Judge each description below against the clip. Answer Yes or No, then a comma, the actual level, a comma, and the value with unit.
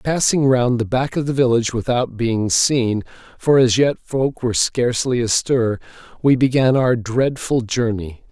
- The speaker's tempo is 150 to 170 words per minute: Yes, average, 160 wpm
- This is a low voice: Yes, low, 120 Hz